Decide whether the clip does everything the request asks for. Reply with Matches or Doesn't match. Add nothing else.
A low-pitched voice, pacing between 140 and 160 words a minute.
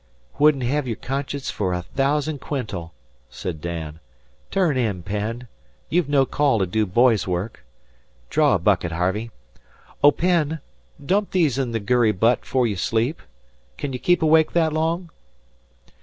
Matches